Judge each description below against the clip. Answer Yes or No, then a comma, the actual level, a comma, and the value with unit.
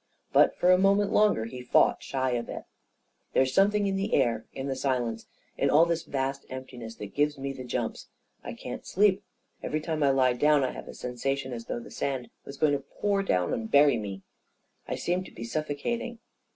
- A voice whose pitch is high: No, low, 135 Hz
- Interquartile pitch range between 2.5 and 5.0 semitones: No, wide, 5.4 semitones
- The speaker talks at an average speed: No, fast, 230 wpm